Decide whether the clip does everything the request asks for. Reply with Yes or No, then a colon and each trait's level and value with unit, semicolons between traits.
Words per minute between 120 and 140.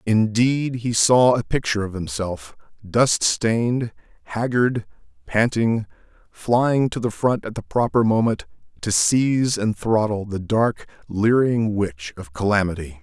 Yes: slow, 135 wpm